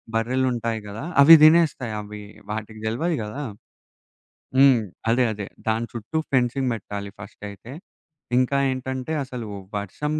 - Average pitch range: Yes, average, 3.6 semitones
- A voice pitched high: No, low, 120 Hz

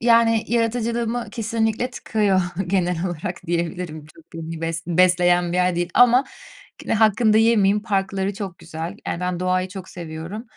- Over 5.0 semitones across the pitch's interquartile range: No, average, 4.3 semitones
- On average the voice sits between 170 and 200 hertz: Yes, high, 190 Hz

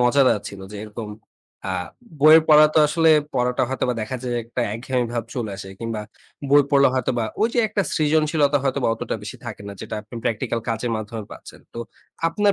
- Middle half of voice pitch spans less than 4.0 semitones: No, average, 4.7 semitones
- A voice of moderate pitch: No, low, 125 Hz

